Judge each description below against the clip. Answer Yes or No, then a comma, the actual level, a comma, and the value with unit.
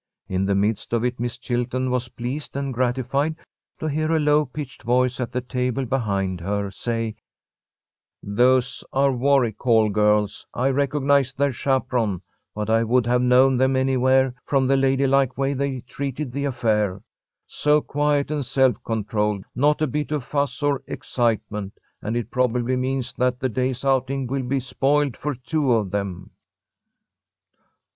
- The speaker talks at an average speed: Yes, average, 160 wpm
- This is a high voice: No, low, 130 Hz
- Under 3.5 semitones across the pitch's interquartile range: Yes, average, 2.9 semitones